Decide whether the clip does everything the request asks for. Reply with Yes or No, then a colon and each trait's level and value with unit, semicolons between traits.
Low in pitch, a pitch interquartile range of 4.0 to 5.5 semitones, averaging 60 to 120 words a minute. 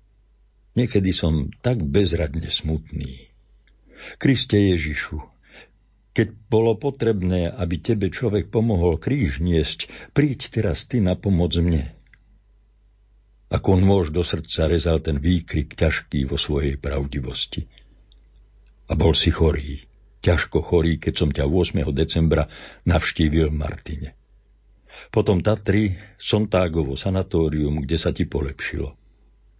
Yes: very low, 90 Hz; average, 4.9 semitones; slow, 110 wpm